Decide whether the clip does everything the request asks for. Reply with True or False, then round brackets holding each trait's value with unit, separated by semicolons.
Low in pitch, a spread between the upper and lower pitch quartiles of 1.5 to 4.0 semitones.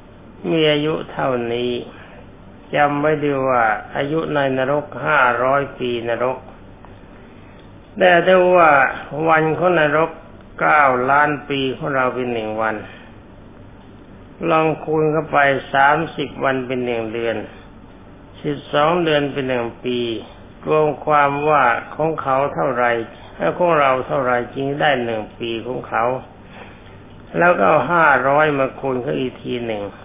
False (130 Hz; 4.6 semitones)